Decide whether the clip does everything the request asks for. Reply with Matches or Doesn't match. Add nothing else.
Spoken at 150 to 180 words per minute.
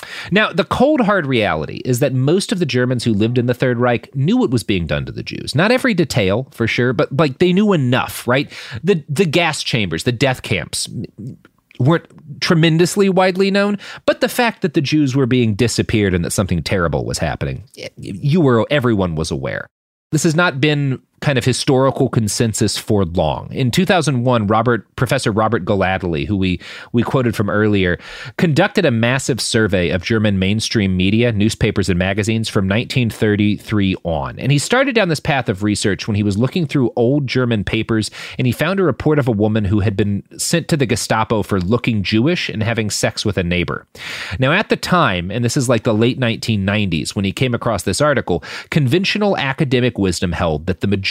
Doesn't match